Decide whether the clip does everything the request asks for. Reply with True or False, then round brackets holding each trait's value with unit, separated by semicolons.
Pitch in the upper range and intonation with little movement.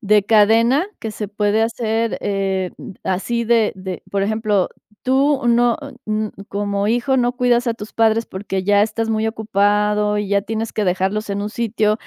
True (215 Hz; 2.1 semitones)